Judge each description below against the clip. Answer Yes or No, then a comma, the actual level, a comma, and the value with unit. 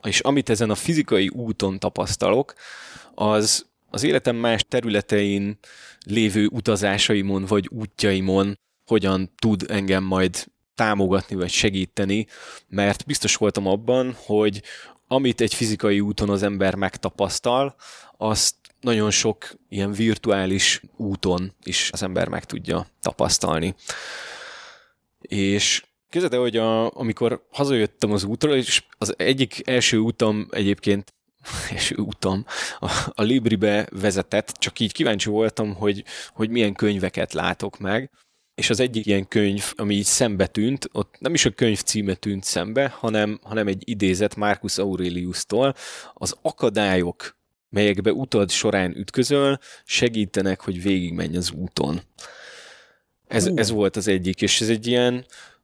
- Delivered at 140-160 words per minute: No, average, 130 wpm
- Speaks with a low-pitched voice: Yes, low, 105 Hz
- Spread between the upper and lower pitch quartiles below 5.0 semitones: Yes, narrow, 2.6 semitones